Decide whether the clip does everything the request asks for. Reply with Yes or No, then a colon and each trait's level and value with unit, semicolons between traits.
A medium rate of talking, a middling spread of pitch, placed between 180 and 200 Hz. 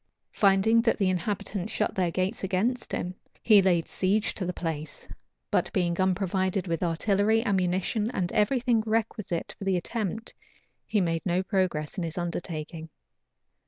Yes: average, 155 wpm; average, 3.3 semitones; high, 190 Hz